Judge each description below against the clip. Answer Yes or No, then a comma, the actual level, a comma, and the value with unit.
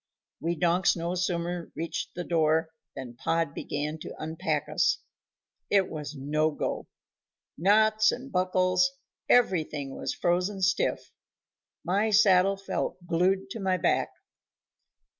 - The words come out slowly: Yes, slow, 120 wpm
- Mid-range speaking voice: Yes, medium, 175 Hz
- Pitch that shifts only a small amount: No, average, 3.1 semitones